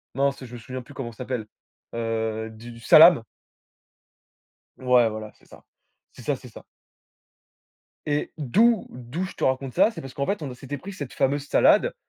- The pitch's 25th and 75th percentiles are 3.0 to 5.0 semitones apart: Yes, average, 3.6 semitones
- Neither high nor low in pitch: No, low, 130 Hz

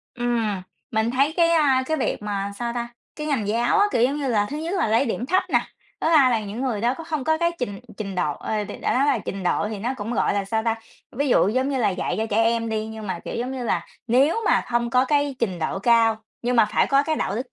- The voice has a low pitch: No, high, 240 Hz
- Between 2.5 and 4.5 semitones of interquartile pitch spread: Yes, average, 4.2 semitones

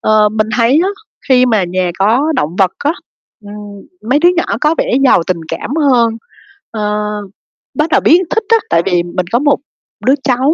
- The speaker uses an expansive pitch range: Yes, wide, 6.2 semitones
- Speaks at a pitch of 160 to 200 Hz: No, high, 225 Hz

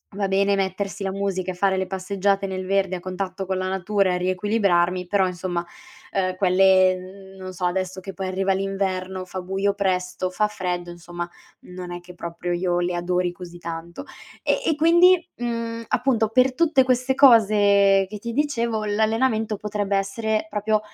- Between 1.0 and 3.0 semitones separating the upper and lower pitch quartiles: Yes, narrow, 2.4 semitones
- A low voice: No, high, 195 Hz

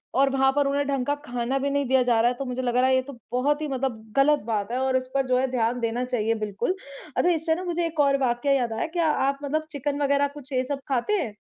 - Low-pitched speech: No, very high, 270 Hz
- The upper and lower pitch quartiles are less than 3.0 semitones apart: Yes, narrow, 2.5 semitones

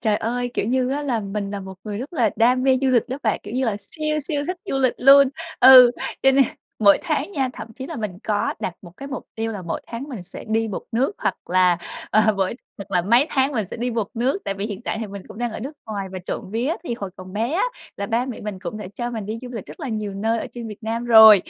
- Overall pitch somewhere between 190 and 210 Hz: No, high, 225 Hz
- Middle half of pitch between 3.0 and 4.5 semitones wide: Yes, average, 3.9 semitones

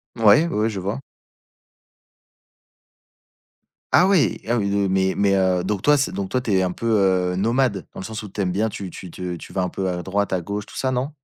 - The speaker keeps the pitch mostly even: No, average, 3.1 semitones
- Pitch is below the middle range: Yes, low, 100 Hz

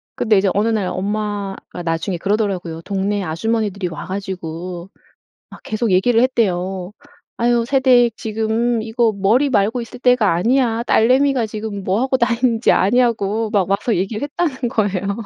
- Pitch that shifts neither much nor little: Yes, average, 3.6 semitones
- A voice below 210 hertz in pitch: No, high, 215 Hz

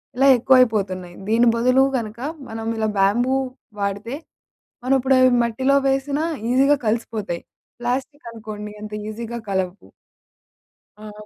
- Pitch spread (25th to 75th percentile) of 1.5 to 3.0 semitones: No, average, 3.6 semitones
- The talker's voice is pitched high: Yes, high, 230 Hz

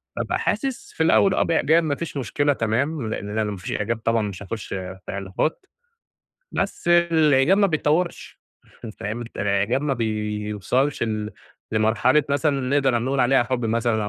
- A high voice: No, low, 120 Hz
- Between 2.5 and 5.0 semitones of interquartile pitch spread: No, wide, 5.5 semitones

